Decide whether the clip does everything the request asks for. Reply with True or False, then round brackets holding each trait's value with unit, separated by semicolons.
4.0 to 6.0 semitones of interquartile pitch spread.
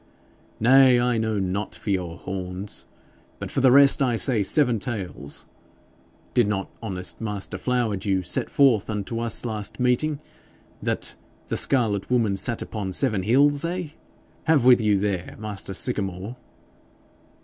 True (4.3 semitones)